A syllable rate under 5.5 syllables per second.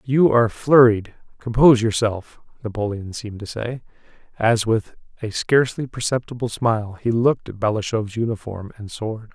Yes: 5.2 syllables/s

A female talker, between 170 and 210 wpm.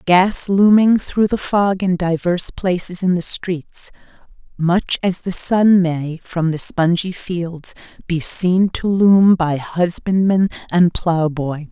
No: female; average, 145 wpm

